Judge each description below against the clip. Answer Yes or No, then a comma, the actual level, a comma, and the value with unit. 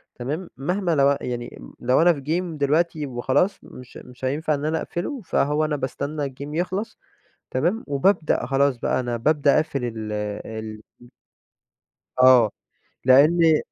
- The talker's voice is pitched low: No, medium, 145 Hz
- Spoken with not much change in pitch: No, average, 4.1 semitones